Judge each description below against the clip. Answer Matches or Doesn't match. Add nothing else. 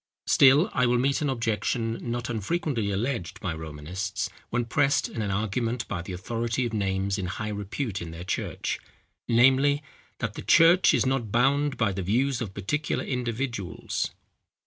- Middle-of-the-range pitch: Doesn't match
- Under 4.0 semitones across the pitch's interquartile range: Doesn't match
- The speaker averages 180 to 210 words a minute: Doesn't match